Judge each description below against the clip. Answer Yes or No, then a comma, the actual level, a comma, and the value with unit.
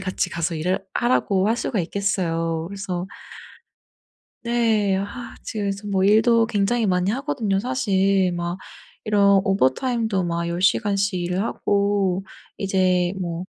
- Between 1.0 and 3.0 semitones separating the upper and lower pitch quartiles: Yes, narrow, 2.5 semitones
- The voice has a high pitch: Yes, high, 195 Hz